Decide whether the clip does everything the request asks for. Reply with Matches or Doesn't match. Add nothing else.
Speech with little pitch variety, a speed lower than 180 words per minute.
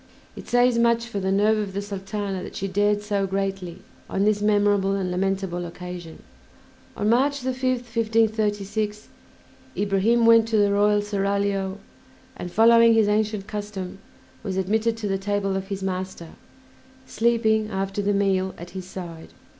Matches